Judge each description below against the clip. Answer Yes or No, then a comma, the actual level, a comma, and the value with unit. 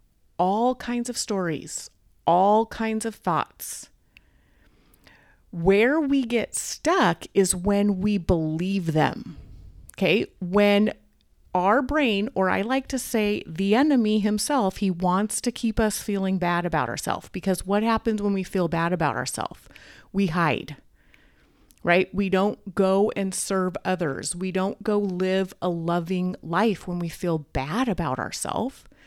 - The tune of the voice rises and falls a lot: No, average, 3.0 semitones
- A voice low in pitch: No, high, 195 Hz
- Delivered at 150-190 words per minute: No, average, 140 wpm